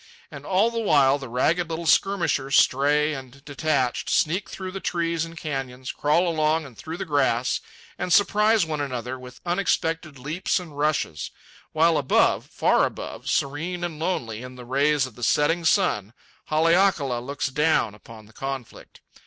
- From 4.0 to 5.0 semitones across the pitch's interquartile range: Yes, average, 4.3 semitones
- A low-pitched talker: No, medium, 150 Hz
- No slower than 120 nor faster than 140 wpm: No, average, 160 wpm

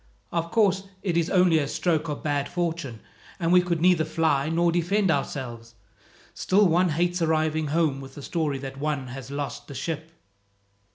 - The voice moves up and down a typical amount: Yes, average, 3.5 semitones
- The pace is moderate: Yes, average, 175 wpm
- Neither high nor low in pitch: Yes, medium, 160 Hz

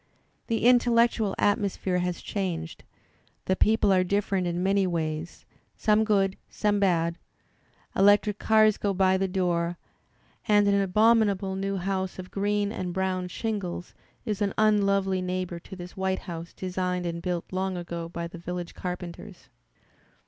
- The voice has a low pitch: No, high, 190 Hz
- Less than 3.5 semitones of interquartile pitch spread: Yes, narrow, 2.4 semitones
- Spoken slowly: No, average, 145 wpm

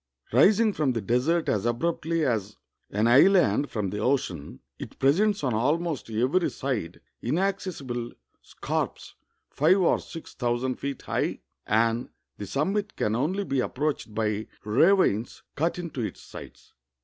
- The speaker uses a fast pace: No, average, 145 wpm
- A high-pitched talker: No, low, 135 Hz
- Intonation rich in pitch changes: Yes, wide, 6.8 semitones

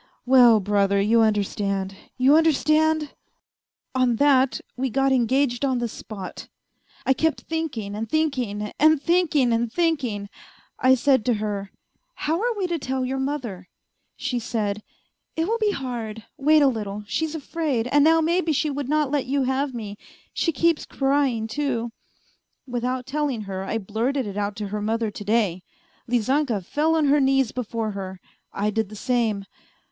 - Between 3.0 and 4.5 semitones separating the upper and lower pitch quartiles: No, wide, 5.4 semitones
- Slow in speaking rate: No, average, 170 wpm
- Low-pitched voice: No, very high, 255 Hz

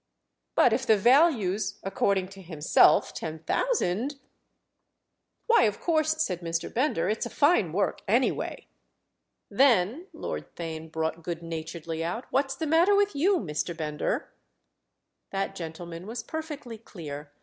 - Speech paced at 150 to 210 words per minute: No, slow, 135 wpm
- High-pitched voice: Yes, high, 200 Hz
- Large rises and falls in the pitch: Yes, wide, 8.9 semitones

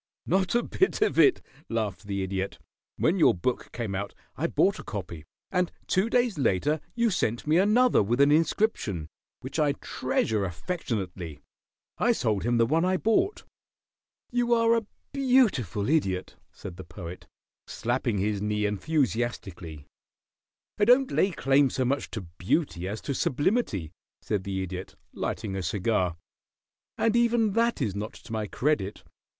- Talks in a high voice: No, low, 120 Hz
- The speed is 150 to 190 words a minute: Yes, average, 155 wpm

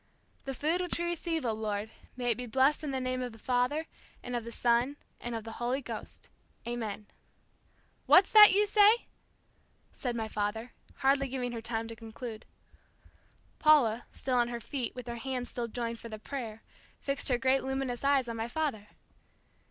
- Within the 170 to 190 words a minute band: Yes, average, 185 wpm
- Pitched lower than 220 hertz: No, high, 245 Hz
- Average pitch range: Yes, average, 3.1 semitones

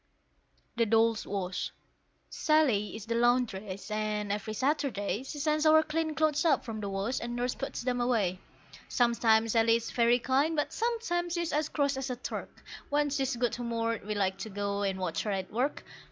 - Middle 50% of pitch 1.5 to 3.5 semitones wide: No, average, 5.2 semitones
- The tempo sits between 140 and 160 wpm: No, average, 185 wpm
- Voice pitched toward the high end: Yes, high, 235 Hz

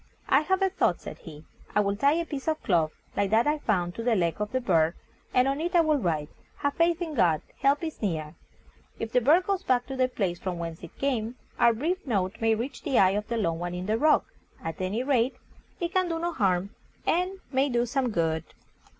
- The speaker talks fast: Yes, fast, 235 wpm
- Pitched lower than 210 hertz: No, high, 235 Hz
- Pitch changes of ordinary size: No, wide, 8.2 semitones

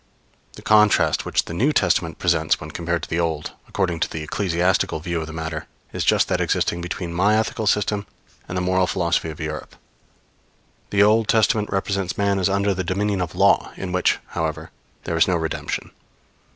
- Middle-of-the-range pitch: No, very low, 90 Hz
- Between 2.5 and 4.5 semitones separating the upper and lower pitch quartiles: Yes, average, 3.2 semitones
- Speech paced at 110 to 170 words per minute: No, average, 190 wpm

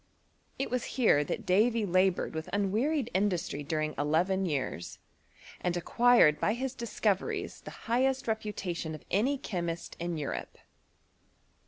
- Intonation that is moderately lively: No, wide, 5.9 semitones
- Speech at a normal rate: No, slow, 130 wpm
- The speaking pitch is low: No, high, 190 Hz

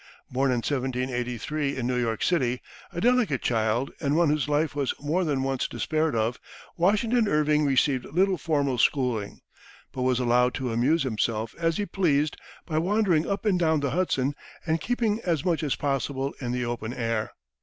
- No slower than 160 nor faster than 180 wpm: Yes, average, 175 wpm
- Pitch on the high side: No, medium, 140 Hz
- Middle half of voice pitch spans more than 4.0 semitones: Yes, average, 4.9 semitones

